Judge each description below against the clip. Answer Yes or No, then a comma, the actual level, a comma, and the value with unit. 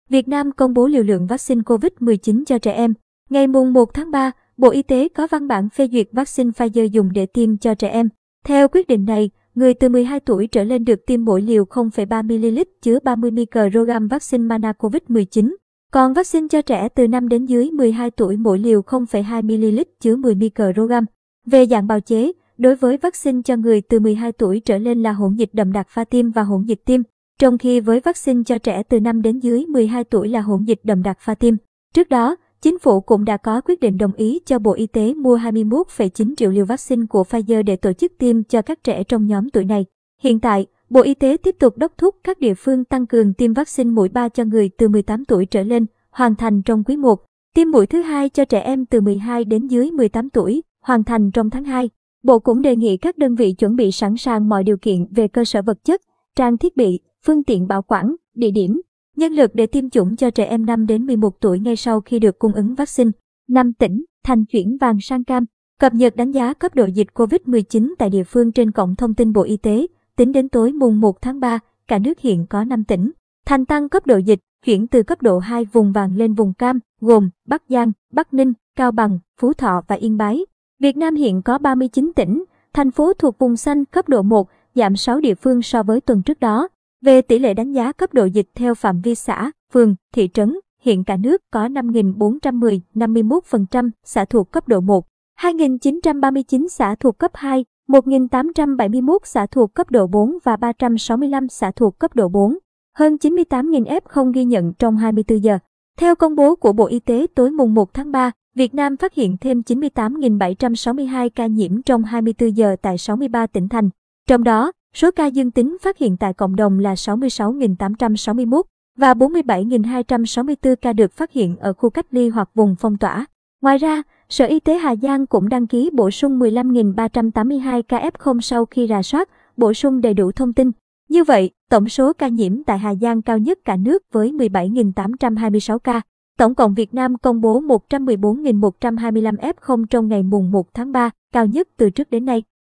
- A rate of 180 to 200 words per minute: No, average, 210 wpm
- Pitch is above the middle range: Yes, high, 235 Hz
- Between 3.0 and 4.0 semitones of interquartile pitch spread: Yes, average, 3.3 semitones